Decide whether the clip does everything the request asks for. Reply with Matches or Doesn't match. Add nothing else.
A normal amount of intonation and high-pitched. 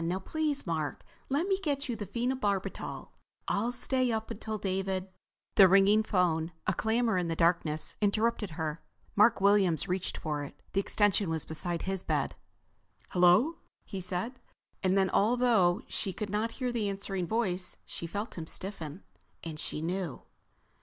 Matches